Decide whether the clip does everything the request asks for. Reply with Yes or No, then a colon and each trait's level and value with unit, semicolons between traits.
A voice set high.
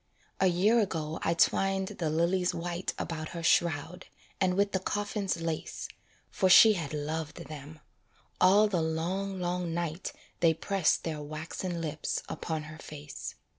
No: medium, 170 Hz